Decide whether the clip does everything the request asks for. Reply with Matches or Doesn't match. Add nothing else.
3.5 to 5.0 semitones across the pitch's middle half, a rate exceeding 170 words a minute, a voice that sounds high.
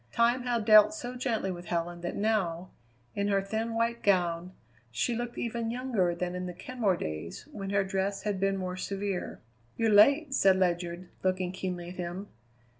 Matches